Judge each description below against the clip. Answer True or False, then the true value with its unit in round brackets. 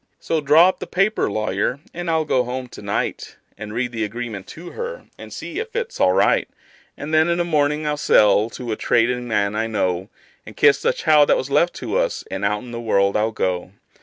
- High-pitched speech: False (125 Hz)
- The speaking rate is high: True (225 wpm)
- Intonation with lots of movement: True (7.0 semitones)